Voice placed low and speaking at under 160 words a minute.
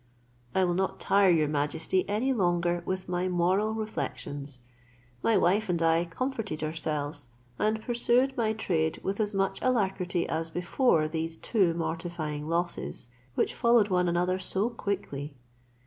No: medium, 180 Hz; average, 145 wpm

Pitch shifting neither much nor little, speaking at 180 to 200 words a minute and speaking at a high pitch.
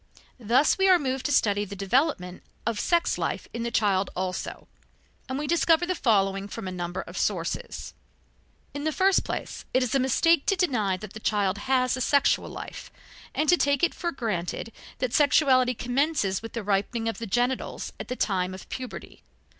No: wide, 6.1 semitones; average, 190 wpm; high, 245 Hz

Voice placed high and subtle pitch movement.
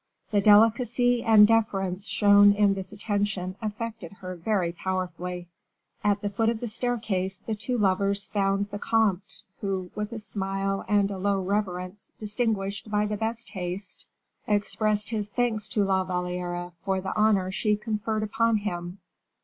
Yes: high, 205 Hz; narrow, 2.2 semitones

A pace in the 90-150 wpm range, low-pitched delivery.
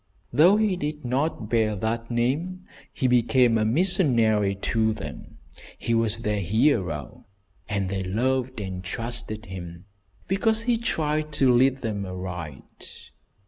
Yes: slow, 135 wpm; low, 115 Hz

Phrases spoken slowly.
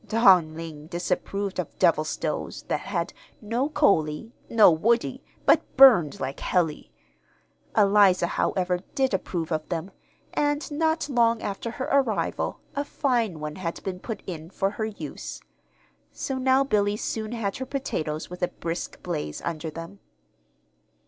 No: average, 145 wpm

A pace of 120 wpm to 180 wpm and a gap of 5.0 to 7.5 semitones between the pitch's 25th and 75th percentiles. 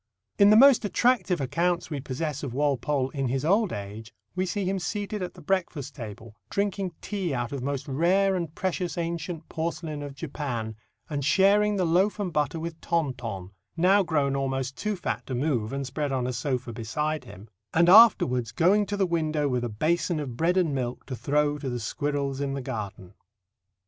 No: average, 195 wpm; wide, 5.5 semitones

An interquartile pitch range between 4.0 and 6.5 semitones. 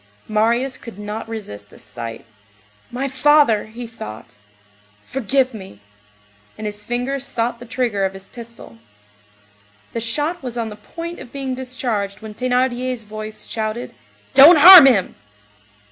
No: average, 3.6 semitones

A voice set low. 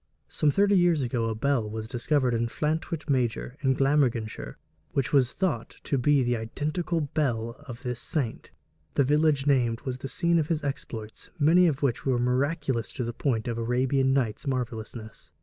Yes: low, 130 Hz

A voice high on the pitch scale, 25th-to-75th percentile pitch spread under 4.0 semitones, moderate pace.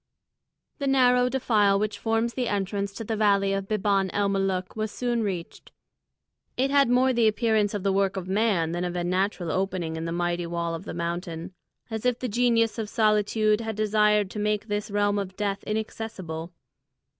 Yes: high, 205 Hz; average, 2.9 semitones; average, 190 wpm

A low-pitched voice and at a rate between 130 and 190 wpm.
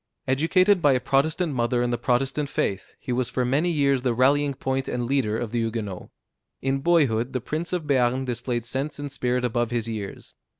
No: low, 130 Hz; average, 200 wpm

